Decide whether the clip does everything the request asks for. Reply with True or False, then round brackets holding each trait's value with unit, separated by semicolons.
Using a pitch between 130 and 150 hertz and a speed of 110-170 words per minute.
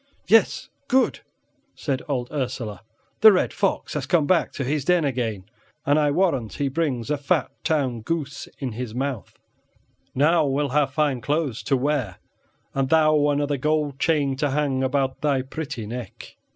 True (140 Hz; 165 wpm)